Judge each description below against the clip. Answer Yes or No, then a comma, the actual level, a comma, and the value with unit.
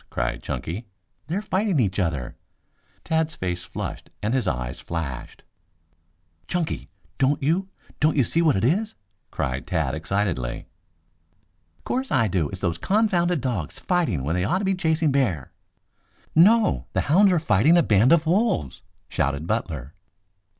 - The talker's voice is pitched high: No, low, 125 Hz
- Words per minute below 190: Yes, average, 150 wpm